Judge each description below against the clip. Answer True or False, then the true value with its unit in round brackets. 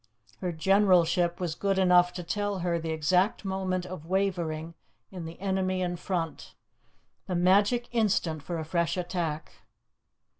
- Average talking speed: True (145 wpm)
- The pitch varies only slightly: True (2.2 semitones)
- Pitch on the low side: False (180 Hz)